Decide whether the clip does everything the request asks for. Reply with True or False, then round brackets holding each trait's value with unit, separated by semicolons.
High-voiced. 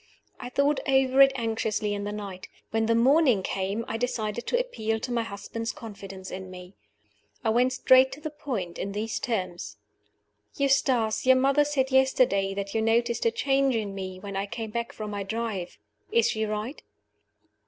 True (225 Hz)